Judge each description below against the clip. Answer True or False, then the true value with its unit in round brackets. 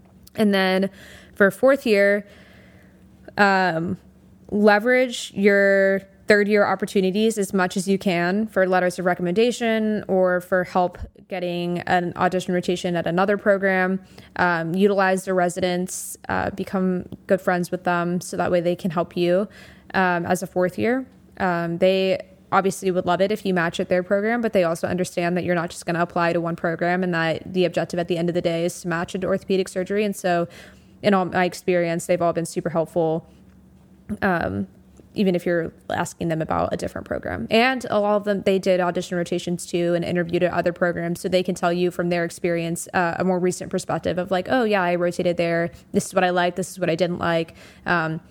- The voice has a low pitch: False (180 Hz)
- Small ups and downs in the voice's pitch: True (1.8 semitones)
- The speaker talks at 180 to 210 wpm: True (200 wpm)